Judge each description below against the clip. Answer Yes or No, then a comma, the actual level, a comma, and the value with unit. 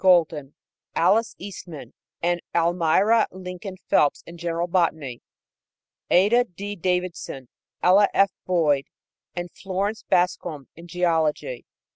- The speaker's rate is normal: No, slow, 105 wpm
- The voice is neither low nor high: Yes, medium, 175 Hz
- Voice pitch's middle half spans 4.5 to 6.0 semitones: No, narrow, 2.6 semitones